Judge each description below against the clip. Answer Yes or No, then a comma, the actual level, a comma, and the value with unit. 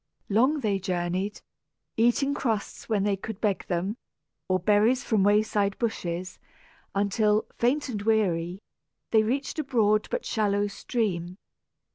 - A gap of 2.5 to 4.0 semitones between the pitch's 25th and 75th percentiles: Yes, average, 2.8 semitones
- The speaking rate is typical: No, slow, 130 wpm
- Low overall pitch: No, high, 210 Hz